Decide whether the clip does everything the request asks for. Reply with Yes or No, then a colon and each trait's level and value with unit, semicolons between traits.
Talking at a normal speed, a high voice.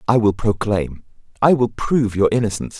No: average, 170 wpm; low, 105 Hz